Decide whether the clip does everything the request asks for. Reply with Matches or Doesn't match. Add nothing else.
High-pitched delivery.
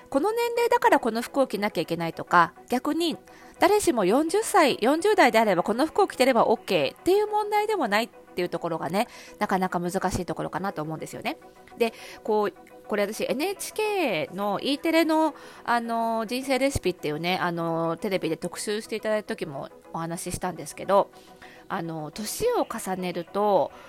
Matches